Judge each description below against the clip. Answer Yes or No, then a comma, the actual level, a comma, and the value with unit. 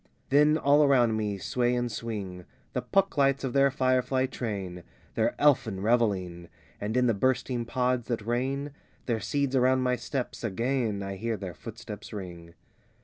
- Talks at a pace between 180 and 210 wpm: No, average, 165 wpm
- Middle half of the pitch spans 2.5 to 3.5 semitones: No, average, 4.0 semitones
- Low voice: Yes, low, 120 Hz